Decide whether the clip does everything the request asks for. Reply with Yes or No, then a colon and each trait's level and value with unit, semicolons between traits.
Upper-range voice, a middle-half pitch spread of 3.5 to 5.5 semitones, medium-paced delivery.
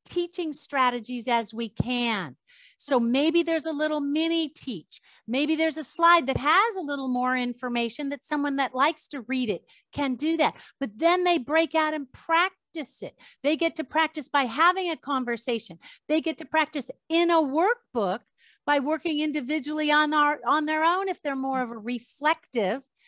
Yes: very high, 300 Hz; average, 3.8 semitones; average, 180 wpm